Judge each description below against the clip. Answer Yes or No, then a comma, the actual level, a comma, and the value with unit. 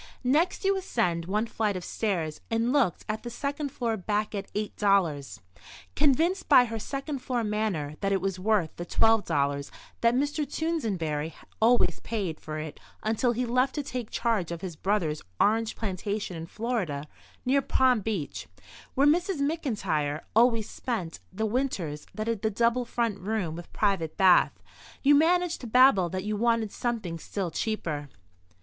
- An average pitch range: No, wide, 5.7 semitones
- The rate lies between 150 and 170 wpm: Yes, average, 160 wpm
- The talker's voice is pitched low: No, high, 215 Hz